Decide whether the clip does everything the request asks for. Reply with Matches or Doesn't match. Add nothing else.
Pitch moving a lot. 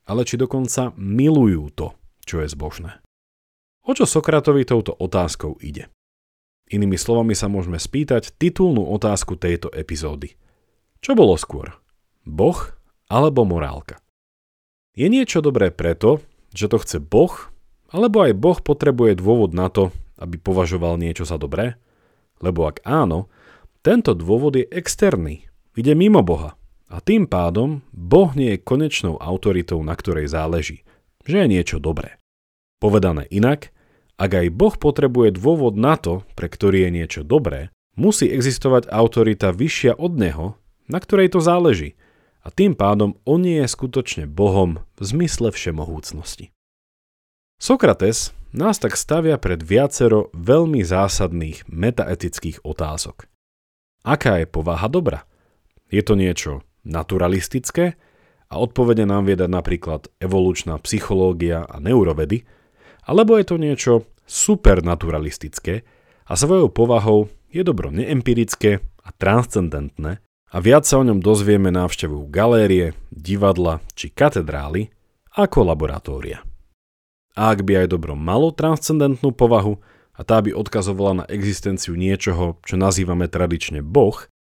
Matches